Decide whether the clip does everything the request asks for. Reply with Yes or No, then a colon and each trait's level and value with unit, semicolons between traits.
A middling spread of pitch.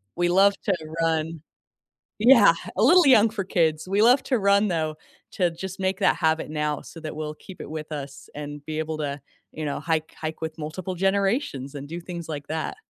Yes: average, 3.9 semitones